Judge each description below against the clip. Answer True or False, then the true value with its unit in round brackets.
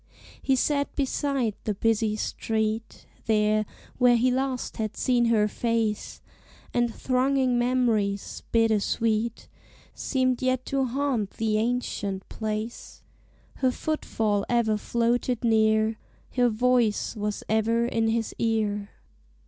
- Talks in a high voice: True (230 Hz)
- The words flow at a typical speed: False (115 wpm)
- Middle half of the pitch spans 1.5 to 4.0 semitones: True (2.6 semitones)